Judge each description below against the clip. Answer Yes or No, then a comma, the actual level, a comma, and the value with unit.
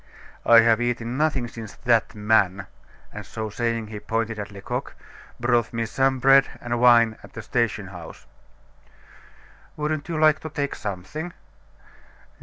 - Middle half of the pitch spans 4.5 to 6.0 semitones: No, average, 3.4 semitones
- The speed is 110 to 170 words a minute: Yes, average, 145 wpm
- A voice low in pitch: Yes, low, 115 Hz